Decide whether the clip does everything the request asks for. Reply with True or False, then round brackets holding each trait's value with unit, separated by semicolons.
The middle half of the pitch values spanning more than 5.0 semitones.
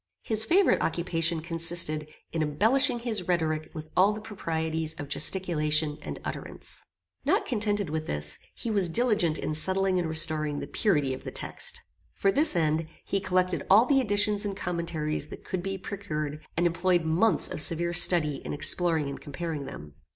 False (4.2 semitones)